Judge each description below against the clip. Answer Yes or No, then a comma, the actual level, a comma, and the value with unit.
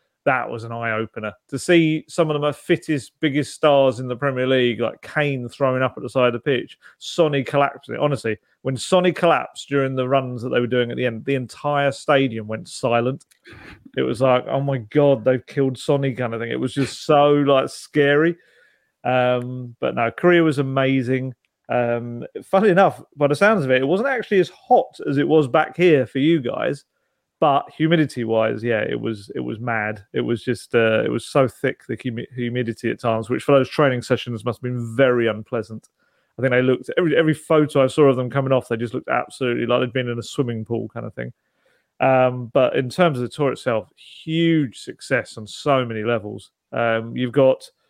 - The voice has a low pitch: Yes, low, 130 Hz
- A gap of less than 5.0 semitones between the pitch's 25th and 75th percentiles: Yes, average, 3.6 semitones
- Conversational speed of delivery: No, fast, 210 wpm